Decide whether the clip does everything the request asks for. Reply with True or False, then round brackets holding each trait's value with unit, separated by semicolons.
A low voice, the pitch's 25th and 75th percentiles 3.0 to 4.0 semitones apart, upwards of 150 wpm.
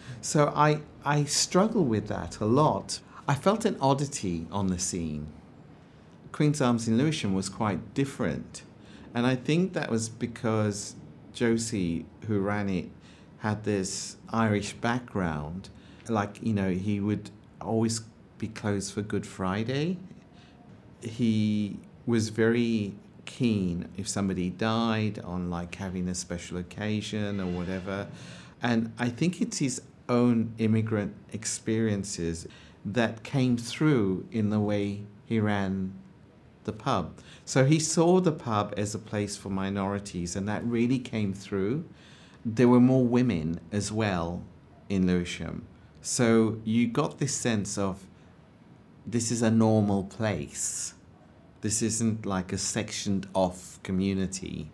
False (105 Hz; 3.6 semitones; 135 wpm)